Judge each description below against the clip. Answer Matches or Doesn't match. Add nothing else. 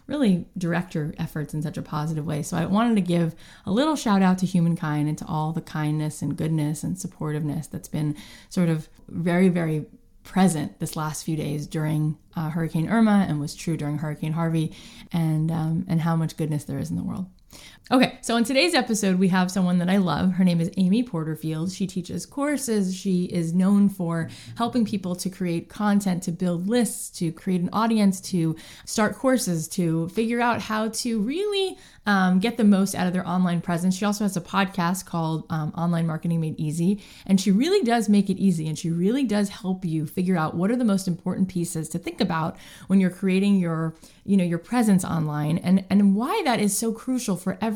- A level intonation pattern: Doesn't match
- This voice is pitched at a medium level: Matches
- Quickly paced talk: Matches